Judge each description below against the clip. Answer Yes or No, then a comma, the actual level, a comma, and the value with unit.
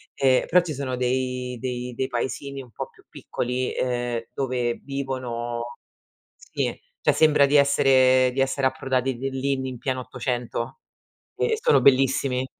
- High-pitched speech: No, low, 130 Hz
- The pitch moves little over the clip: Yes, narrow, 1.5 semitones